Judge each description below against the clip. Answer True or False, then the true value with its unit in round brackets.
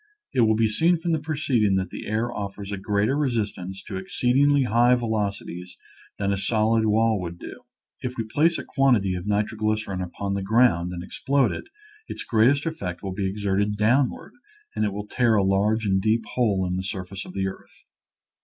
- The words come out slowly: False (195 wpm)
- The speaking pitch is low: True (105 Hz)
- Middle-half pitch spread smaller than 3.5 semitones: False (3.8 semitones)